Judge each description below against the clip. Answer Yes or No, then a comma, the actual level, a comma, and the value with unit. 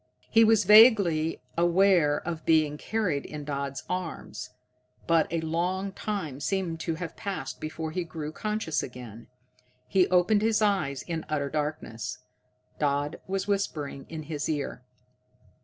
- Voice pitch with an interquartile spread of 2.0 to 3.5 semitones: No, average, 4.4 semitones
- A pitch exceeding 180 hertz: No, medium, 165 Hz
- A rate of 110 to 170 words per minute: Yes, average, 140 wpm